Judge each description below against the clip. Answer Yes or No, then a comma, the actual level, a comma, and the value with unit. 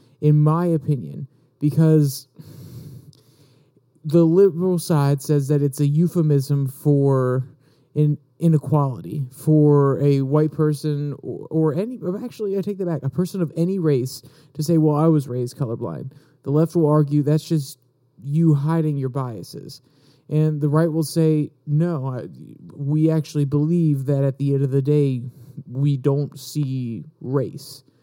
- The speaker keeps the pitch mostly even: Yes, narrow, 2.3 semitones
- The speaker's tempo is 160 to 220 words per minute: No, average, 150 wpm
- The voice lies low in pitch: No, medium, 150 Hz